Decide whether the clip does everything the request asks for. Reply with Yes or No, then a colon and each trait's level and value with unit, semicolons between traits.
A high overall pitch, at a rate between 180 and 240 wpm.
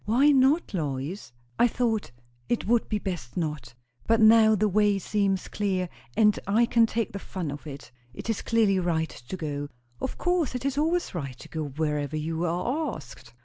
Yes: high, 195 Hz; average, 190 wpm